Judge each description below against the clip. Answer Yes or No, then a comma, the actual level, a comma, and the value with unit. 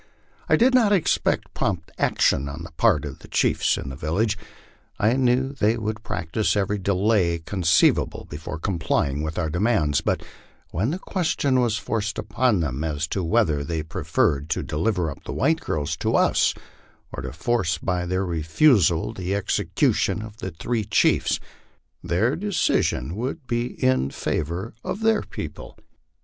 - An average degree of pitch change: No, wide, 6.5 semitones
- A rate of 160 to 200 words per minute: Yes, average, 165 wpm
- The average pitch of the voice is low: Yes, very low, 95 Hz